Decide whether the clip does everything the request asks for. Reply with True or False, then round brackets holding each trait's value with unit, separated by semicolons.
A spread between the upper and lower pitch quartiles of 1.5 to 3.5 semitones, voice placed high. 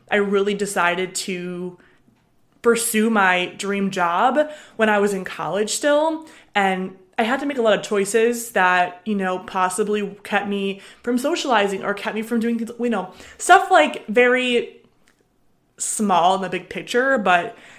False (4.0 semitones; 205 Hz)